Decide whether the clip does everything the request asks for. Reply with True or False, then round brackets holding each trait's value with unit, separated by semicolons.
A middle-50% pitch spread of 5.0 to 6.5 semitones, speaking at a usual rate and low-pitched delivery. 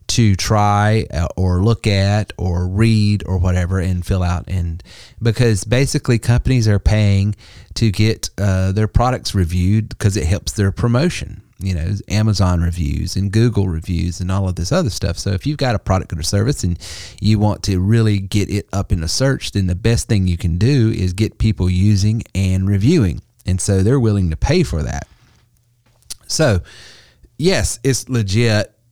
False (3.5 semitones; 180 wpm; 100 Hz)